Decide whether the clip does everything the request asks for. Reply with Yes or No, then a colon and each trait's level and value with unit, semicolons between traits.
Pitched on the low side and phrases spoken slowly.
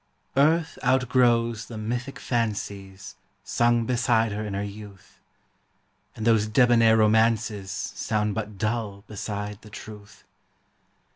Yes: low, 110 Hz; slow, 115 wpm